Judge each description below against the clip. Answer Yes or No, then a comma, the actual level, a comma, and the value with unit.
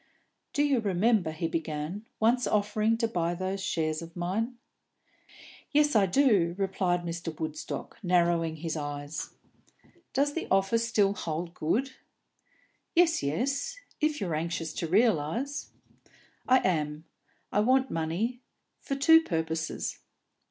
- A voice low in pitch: No, high, 190 Hz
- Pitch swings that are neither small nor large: No, wide, 6.5 semitones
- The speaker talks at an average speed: No, slow, 125 wpm